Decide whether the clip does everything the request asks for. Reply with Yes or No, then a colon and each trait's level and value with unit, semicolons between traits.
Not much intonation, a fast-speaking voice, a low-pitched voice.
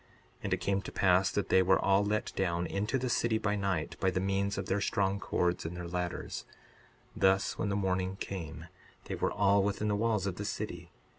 Yes: narrow, 1.7 semitones; fast, 220 wpm; very low, 95 Hz